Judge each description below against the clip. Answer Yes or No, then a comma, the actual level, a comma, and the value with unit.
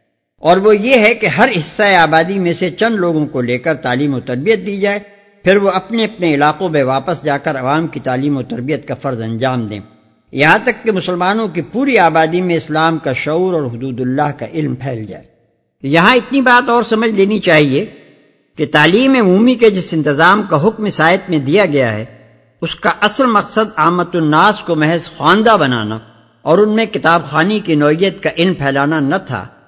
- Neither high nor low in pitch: Yes, medium, 165 Hz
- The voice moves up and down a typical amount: No, wide, 6.2 semitones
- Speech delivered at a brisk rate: Yes, fast, 200 wpm